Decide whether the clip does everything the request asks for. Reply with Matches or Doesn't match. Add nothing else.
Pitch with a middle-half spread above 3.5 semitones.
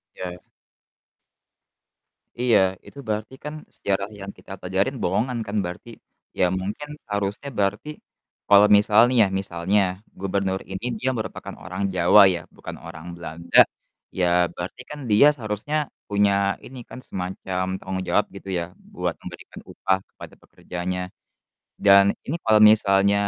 Doesn't match